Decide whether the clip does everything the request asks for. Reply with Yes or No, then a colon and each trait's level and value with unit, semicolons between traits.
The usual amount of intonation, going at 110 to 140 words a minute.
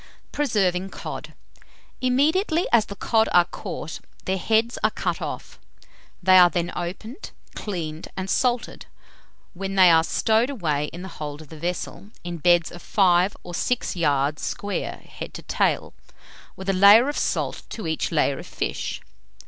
No: average, 4.5 semitones; average, 160 wpm